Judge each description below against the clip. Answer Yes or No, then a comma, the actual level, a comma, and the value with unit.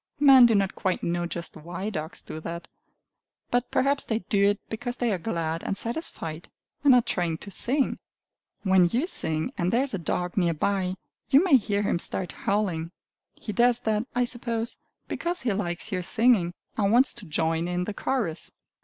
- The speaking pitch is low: No, high, 200 Hz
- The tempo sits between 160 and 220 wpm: Yes, average, 190 wpm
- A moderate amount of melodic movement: No, wide, 5.8 semitones